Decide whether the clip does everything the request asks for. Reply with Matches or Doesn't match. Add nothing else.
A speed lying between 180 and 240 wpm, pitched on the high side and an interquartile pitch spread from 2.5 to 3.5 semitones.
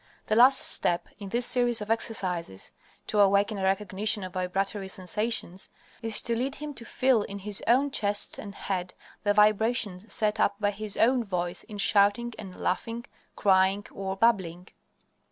Doesn't match